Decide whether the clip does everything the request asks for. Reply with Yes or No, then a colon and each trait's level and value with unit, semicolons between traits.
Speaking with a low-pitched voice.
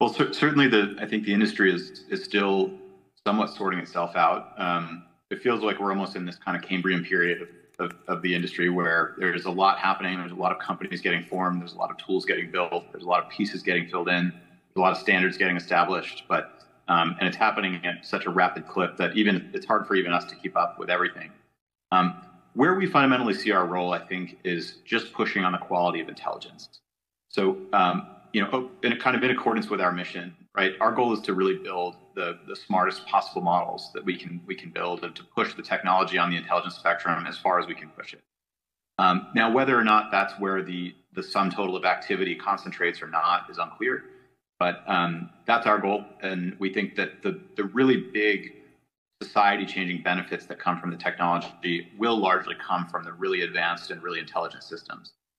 Yes: very low, 95 Hz